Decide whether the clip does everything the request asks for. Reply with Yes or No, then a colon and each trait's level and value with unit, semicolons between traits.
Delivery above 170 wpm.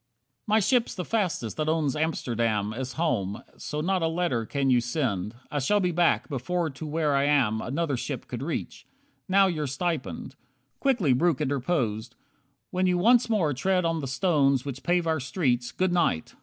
Yes: average, 185 wpm